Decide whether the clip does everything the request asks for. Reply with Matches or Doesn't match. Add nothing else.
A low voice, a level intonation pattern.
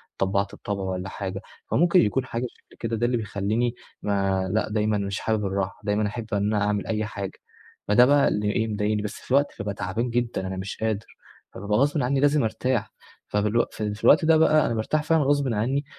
Doesn't match